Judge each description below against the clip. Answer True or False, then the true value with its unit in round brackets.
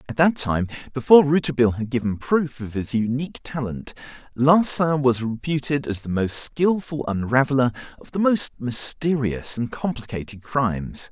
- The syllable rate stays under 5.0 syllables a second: False (5.1 syllables/s)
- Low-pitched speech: True (130 Hz)